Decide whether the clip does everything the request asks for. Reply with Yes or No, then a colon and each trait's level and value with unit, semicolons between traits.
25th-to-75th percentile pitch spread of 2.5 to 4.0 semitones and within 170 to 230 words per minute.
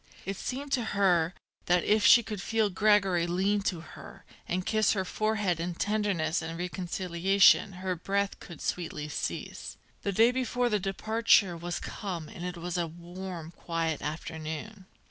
No: average, 3.4 semitones; average, 160 wpm